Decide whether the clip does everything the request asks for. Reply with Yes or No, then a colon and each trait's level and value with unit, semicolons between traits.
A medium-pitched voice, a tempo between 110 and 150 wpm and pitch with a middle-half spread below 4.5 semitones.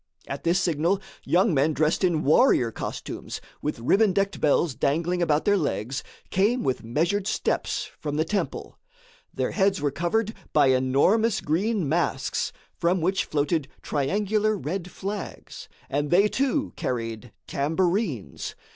No: medium, 170 Hz; average, 140 wpm; wide, 5.6 semitones